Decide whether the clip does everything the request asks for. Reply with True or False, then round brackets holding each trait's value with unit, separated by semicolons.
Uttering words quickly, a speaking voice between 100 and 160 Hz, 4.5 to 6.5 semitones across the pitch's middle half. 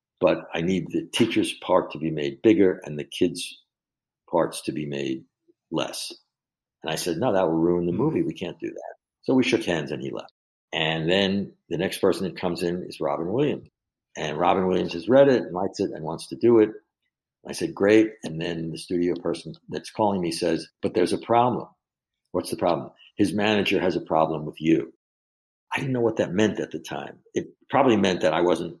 False (215 wpm; 90 Hz; 5.3 semitones)